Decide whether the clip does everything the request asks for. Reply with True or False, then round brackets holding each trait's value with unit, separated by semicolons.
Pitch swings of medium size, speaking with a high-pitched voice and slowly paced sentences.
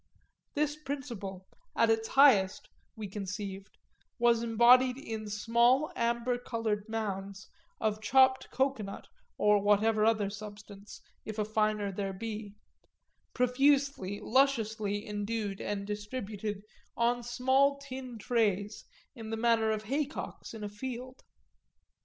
True (3.3 semitones; 220 Hz; 115 wpm)